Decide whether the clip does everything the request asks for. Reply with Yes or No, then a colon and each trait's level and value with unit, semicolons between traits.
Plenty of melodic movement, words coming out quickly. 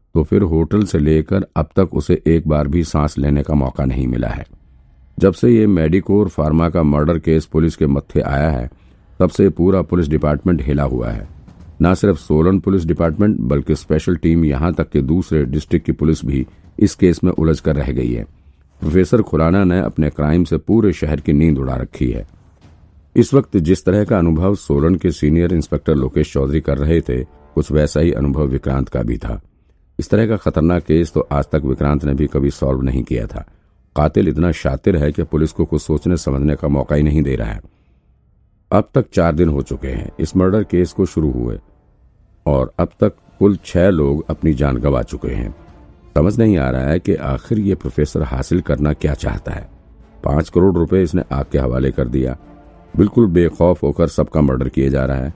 No: average, 3.8 semitones; fast, 205 wpm